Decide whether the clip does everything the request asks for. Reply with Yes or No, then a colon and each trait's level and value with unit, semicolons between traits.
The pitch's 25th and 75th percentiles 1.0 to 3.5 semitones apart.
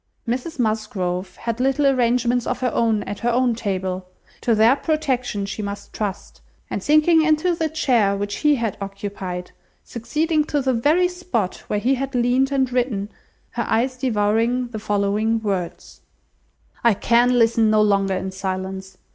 No: average, 4.3 semitones